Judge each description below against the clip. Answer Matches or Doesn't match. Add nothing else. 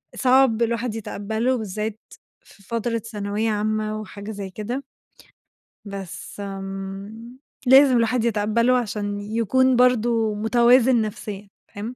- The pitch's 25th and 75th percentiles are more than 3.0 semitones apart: Doesn't match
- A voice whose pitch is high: Matches